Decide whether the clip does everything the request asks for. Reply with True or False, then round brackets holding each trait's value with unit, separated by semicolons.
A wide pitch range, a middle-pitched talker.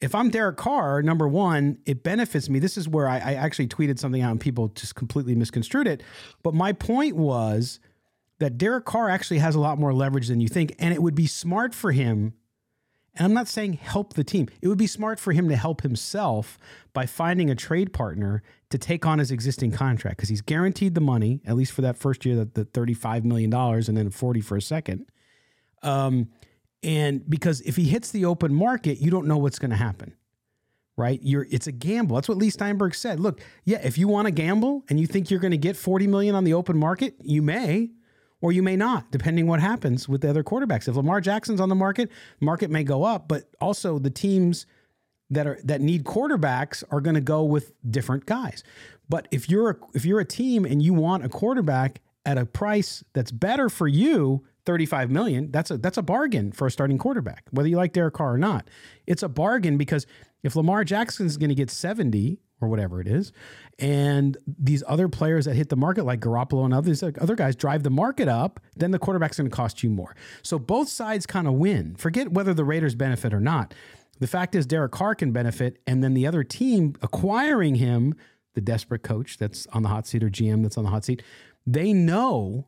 True (6.3 semitones; 150 Hz)